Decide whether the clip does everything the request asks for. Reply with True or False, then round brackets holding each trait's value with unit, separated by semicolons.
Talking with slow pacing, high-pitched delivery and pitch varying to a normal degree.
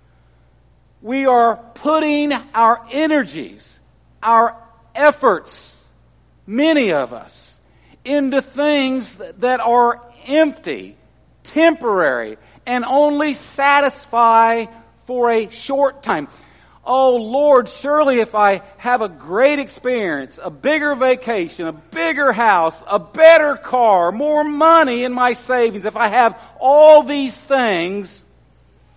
True (110 wpm; 250 Hz; 4.3 semitones)